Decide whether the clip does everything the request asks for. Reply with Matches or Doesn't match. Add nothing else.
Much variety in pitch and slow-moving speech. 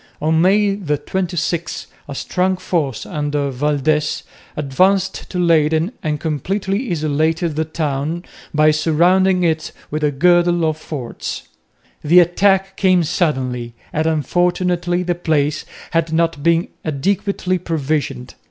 Doesn't match